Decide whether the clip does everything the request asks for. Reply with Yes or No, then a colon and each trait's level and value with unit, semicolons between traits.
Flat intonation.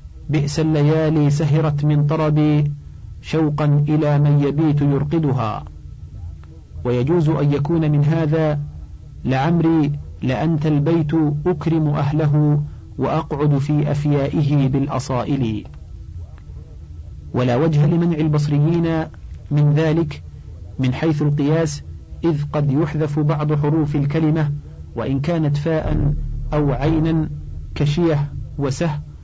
No: average, 3.2 semitones